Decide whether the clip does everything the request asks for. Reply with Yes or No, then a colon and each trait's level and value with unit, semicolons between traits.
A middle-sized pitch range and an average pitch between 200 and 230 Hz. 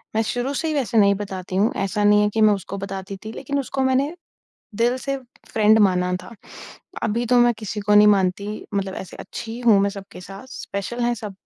Yes: average, 3.4 semitones; high, 210 Hz